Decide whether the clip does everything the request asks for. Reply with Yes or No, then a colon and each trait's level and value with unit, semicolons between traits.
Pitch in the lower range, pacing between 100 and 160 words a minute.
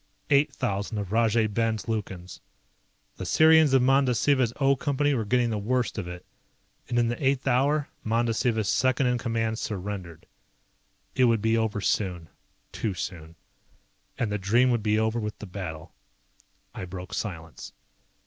Yes: low, 110 Hz; average, 155 wpm